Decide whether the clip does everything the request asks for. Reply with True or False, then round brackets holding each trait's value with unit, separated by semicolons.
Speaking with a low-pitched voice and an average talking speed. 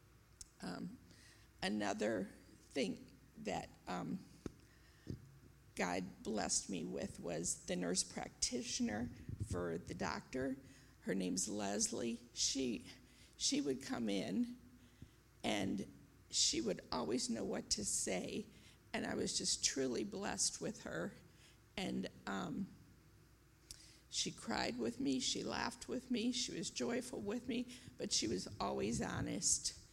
False (120 Hz; 120 wpm)